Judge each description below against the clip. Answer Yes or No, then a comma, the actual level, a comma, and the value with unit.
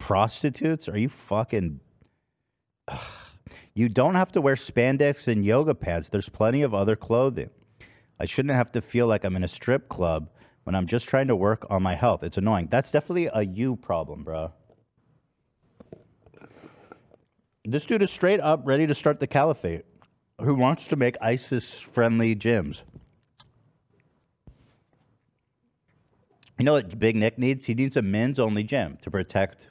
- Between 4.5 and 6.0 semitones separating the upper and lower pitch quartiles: Yes, average, 4.8 semitones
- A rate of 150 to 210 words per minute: Yes, average, 160 wpm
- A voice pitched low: Yes, low, 120 Hz